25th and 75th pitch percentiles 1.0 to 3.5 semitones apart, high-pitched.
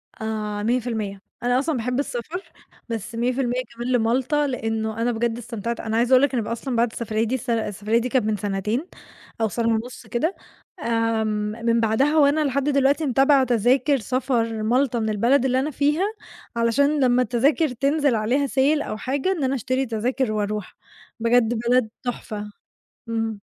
Yes: average, 3.2 semitones; high, 240 Hz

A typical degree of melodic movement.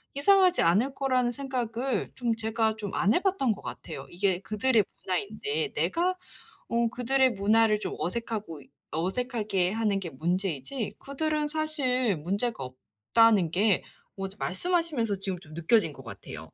No: wide, 5.9 semitones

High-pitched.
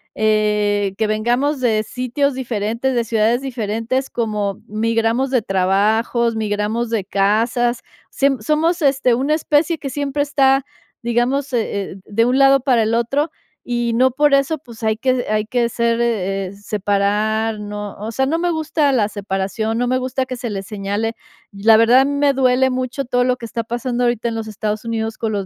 Yes: high, 235 Hz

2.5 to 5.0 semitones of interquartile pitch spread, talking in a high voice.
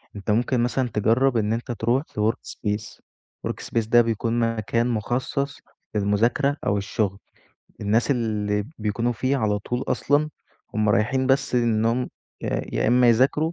No: average, 3.0 semitones; low, 115 Hz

